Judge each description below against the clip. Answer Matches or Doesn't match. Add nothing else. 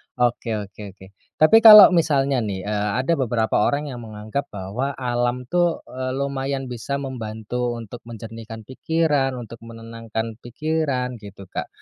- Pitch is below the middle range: Matches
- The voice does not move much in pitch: Doesn't match